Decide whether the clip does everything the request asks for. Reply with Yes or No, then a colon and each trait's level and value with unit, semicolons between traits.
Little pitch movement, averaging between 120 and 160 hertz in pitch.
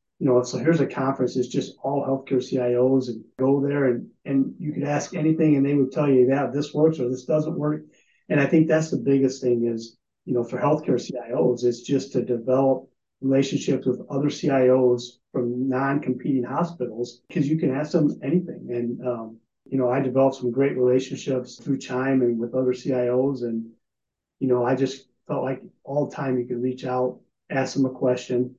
Yes: narrow, 2.1 semitones; low, 130 Hz